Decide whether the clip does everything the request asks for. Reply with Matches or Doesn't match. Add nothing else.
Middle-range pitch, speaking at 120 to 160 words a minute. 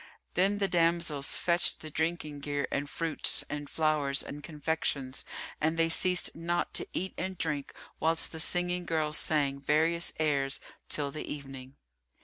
Matches